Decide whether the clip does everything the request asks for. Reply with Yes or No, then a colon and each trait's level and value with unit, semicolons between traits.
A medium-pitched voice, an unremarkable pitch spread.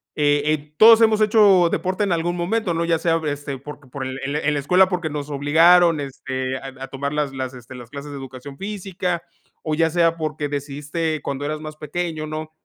Yes: medium, 155 Hz; average, 3.4 semitones